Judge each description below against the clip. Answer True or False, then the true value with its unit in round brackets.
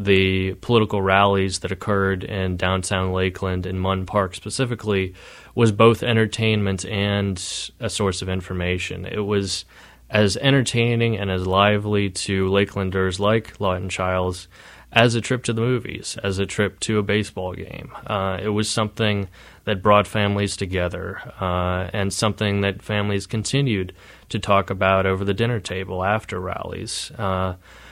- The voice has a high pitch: False (100 Hz)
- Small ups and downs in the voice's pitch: True (2.3 semitones)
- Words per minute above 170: False (150 wpm)